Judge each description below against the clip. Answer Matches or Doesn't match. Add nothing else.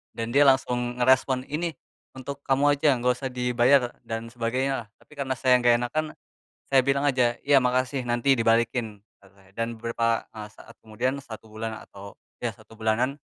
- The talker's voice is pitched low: Matches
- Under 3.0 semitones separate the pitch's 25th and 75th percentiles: Matches